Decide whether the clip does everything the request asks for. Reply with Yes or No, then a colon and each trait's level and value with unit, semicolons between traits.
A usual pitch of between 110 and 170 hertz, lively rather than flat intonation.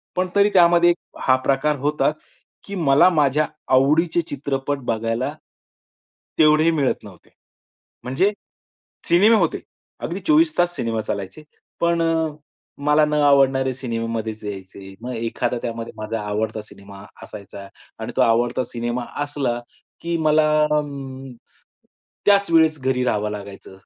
Yes: low, 135 Hz; wide, 6.1 semitones